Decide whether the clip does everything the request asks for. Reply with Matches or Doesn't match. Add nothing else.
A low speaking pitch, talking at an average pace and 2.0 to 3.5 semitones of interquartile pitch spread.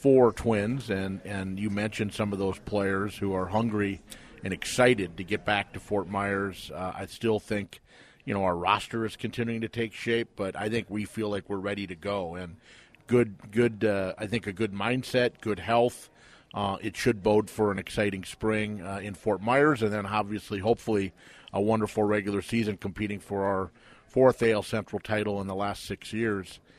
Matches